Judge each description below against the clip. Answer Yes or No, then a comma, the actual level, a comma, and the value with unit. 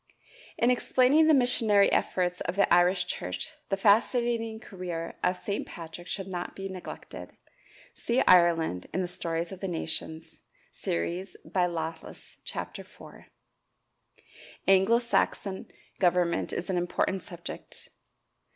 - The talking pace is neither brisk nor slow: No, slow, 125 wpm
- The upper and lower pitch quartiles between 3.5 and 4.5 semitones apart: No, average, 2.8 semitones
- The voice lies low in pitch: No, medium, 185 Hz